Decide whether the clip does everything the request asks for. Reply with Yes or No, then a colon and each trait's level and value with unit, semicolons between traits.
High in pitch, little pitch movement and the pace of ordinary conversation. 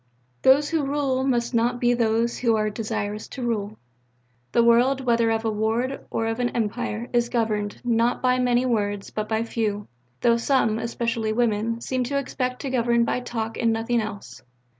Yes: high, 235 Hz; narrow, 2.0 semitones; average, 180 wpm